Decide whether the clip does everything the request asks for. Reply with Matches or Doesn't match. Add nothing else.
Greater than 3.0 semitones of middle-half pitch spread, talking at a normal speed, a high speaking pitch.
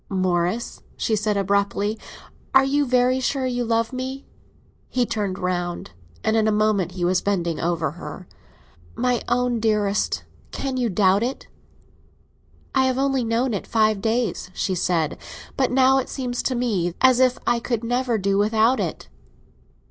Matches